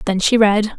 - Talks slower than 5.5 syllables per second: Yes, 4.6 syllables/s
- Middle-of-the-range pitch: No, high, 210 Hz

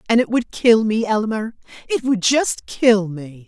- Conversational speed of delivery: Yes, average, 175 wpm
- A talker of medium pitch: No, high, 220 Hz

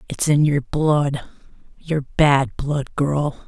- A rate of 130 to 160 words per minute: Yes, average, 140 wpm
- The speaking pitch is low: No, medium, 145 Hz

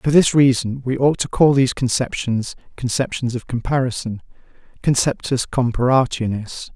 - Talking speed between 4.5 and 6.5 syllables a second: No, 4.1 syllables/s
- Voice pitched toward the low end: Yes, low, 125 Hz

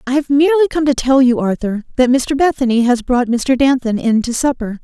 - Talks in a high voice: Yes, very high, 255 Hz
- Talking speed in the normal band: No, fast, 225 wpm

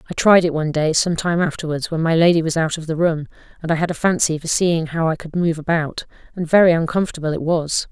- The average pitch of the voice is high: No, medium, 165 Hz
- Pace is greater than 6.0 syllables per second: Yes, 6.2 syllables/s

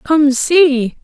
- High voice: Yes, very high, 290 Hz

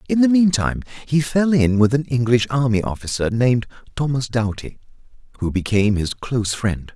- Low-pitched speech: Yes, low, 125 Hz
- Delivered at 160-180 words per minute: Yes, average, 165 wpm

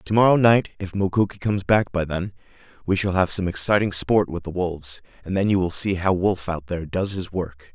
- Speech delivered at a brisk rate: Yes, fast, 230 wpm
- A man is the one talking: Yes, male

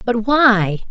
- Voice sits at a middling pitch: No, high, 225 Hz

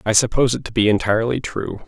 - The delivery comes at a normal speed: No, fast, 225 wpm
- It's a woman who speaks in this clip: No, male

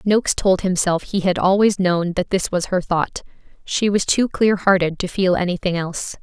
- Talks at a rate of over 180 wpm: Yes, average, 200 wpm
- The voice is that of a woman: Yes, female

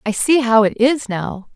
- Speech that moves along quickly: Yes, fast, 230 wpm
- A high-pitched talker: Yes, high, 230 Hz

